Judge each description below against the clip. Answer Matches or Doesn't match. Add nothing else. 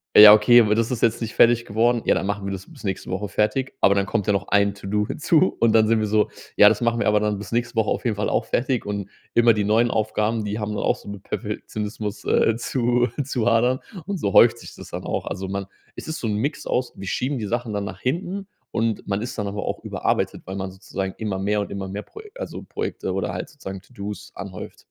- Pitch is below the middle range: Matches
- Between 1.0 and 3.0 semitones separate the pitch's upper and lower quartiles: Matches